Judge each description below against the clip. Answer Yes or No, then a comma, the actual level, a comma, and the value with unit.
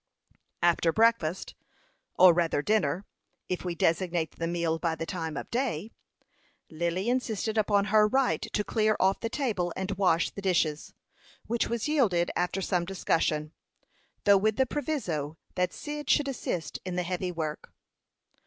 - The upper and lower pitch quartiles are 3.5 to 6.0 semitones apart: Yes, average, 4.5 semitones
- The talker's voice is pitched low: No, medium, 185 Hz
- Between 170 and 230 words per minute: No, average, 155 wpm